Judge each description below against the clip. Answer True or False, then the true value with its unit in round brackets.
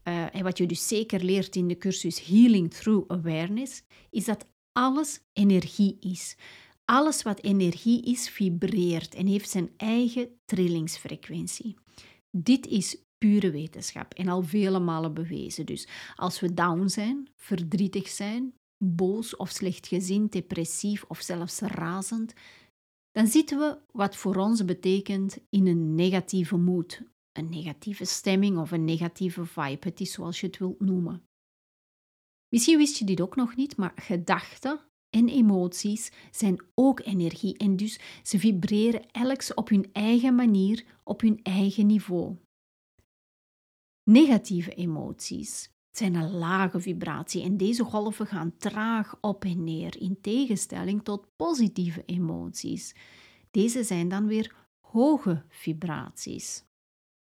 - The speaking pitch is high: True (195 Hz)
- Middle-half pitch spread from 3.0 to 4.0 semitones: True (3.5 semitones)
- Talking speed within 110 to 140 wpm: True (135 wpm)